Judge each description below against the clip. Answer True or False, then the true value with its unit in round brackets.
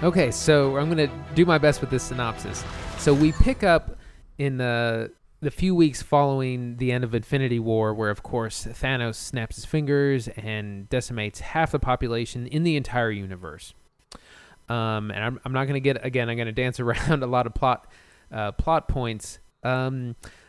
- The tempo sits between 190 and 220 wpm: False (180 wpm)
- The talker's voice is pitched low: True (125 Hz)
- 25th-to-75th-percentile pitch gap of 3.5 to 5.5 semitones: True (4.0 semitones)